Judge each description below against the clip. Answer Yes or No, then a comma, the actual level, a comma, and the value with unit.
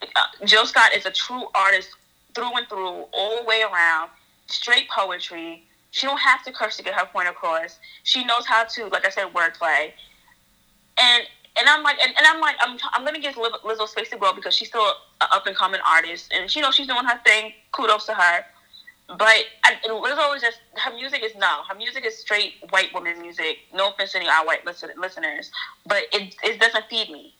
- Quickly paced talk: Yes, fast, 215 wpm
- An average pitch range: Yes, average, 4.7 semitones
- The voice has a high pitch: Yes, high, 220 Hz